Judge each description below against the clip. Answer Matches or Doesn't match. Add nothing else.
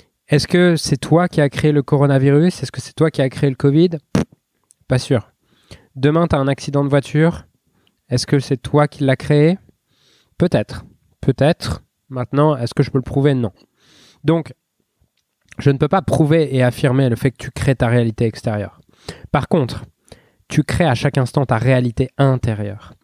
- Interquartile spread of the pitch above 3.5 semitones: Doesn't match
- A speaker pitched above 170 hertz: Doesn't match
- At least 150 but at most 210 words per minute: Matches